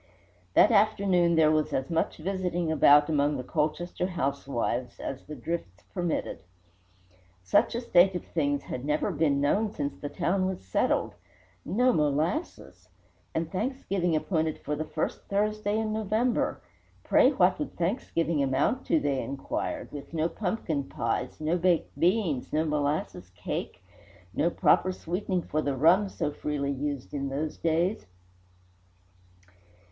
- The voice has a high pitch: No, medium, 160 Hz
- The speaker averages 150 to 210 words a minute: No, average, 140 wpm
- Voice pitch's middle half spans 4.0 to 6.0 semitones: Yes, average, 4.6 semitones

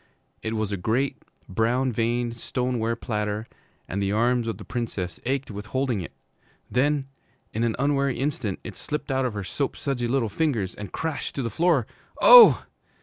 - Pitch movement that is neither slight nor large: Yes, average, 4.0 semitones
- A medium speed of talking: Yes, average, 170 wpm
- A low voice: Yes, low, 120 Hz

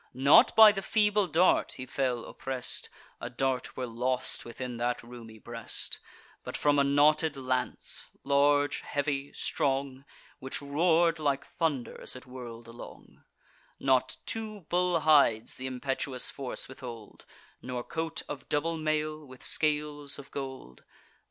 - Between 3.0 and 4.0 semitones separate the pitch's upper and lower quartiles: Yes, average, 3.4 semitones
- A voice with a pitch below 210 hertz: Yes, medium, 140 Hz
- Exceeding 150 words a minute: No, average, 140 wpm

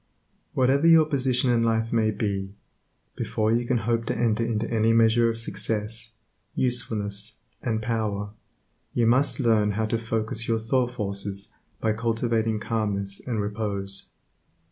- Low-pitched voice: Yes, low, 115 Hz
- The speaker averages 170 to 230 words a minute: No, average, 145 wpm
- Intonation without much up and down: Yes, narrow, 1.8 semitones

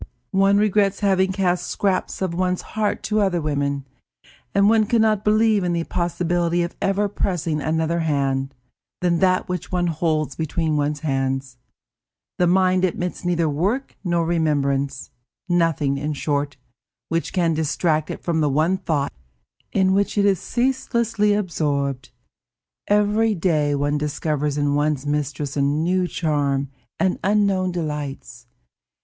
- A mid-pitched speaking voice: Yes, medium, 170 Hz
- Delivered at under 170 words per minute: Yes, average, 145 wpm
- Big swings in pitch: No, average, 4.5 semitones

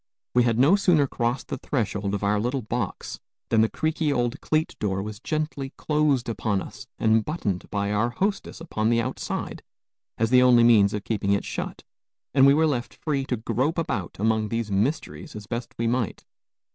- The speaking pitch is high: No, low, 120 Hz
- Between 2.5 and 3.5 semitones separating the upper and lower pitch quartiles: No, average, 4.7 semitones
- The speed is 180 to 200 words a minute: Yes, average, 190 wpm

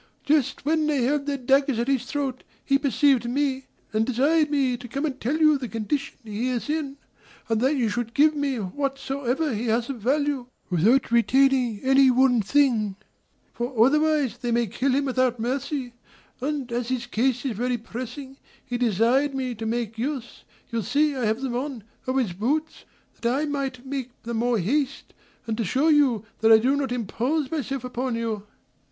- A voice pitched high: Yes, very high, 255 Hz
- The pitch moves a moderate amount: Yes, average, 3.0 semitones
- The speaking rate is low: No, average, 185 wpm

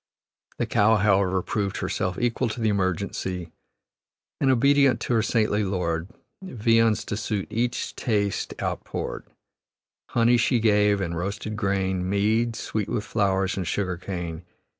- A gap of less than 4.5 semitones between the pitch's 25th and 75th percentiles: Yes, average, 3.2 semitones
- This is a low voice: Yes, low, 105 Hz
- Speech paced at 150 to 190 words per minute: No, average, 140 wpm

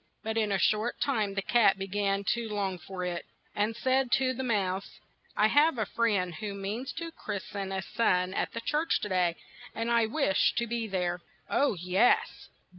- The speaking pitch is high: Yes, high, 210 Hz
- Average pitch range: Yes, average, 3.6 semitones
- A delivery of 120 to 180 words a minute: No, average, 200 wpm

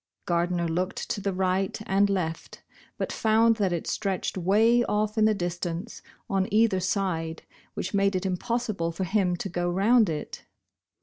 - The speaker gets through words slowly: No, average, 165 wpm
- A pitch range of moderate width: Yes, average, 3.2 semitones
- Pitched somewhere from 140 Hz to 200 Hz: Yes, high, 190 Hz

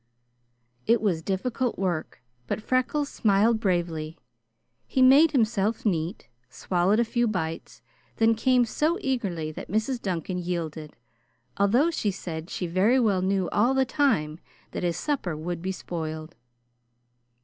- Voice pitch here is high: Yes, high, 195 Hz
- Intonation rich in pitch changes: Yes, wide, 5.8 semitones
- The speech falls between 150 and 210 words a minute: No, average, 140 wpm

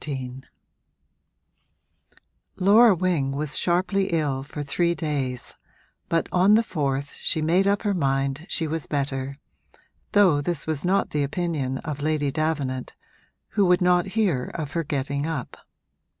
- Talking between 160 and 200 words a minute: No, average, 140 wpm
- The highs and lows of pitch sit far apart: No, average, 4.4 semitones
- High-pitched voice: No, medium, 155 Hz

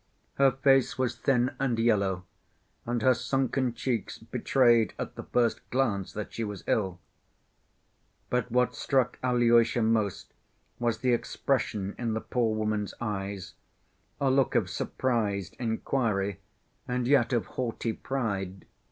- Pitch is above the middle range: No, low, 120 Hz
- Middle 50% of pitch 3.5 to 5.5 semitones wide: No, average, 3.1 semitones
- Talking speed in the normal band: No, slow, 130 wpm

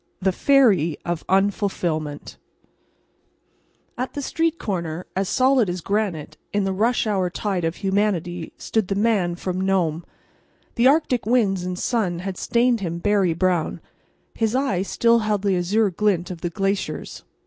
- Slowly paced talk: No, average, 150 wpm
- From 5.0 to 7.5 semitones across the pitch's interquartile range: No, average, 3.7 semitones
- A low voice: No, high, 195 Hz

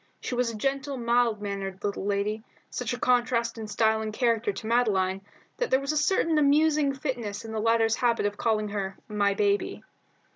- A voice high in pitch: Yes, high, 225 Hz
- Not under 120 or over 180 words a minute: No, average, 190 wpm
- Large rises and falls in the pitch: No, average, 3.3 semitones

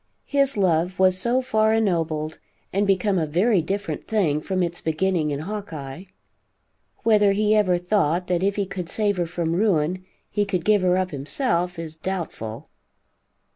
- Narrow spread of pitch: No, average, 3.6 semitones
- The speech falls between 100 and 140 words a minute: No, average, 165 wpm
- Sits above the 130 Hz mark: Yes, medium, 185 Hz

